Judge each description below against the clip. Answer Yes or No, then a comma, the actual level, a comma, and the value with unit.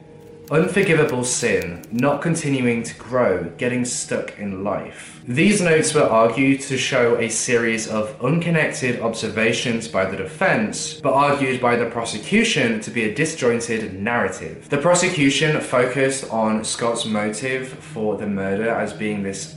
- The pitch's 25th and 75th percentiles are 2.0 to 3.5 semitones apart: No, average, 5.1 semitones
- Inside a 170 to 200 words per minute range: No, average, 140 wpm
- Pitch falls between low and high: No, low, 125 Hz